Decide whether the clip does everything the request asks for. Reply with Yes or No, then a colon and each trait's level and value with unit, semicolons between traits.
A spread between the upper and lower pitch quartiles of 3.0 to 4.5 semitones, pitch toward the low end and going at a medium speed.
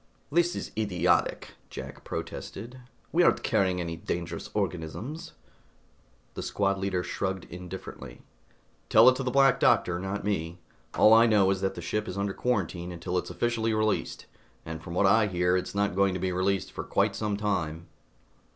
Yes: average, 3.3 semitones; very low, 95 Hz; average, 170 wpm